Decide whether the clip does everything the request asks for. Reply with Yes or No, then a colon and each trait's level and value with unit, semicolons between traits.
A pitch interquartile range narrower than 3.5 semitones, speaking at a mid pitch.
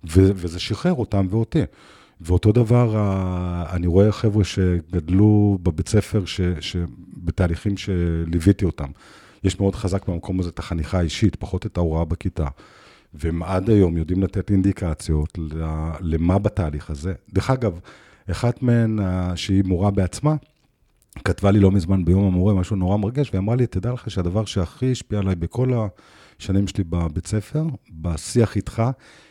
No: average, 3.0 semitones; very low, 95 Hz